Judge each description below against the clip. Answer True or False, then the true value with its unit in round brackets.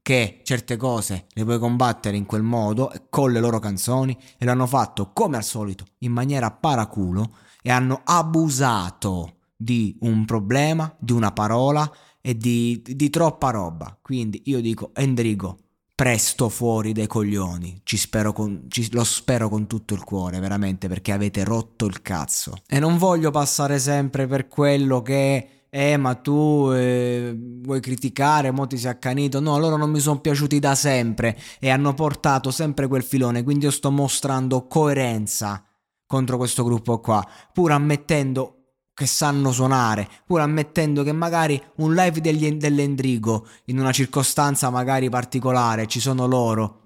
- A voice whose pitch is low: True (125 Hz)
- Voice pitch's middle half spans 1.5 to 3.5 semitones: False (4.1 semitones)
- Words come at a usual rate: True (155 wpm)